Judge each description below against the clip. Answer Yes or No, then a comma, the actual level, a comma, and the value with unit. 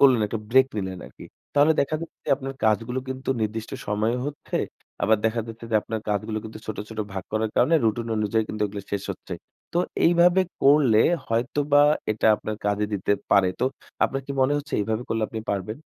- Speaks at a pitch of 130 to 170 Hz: No, low, 115 Hz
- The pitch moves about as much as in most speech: Yes, average, 4.1 semitones